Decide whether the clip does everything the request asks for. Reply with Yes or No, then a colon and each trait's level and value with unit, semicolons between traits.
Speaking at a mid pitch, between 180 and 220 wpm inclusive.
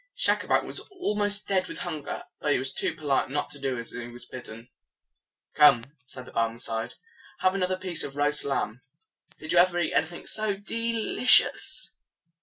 Yes: medium, 150 Hz; average, 185 wpm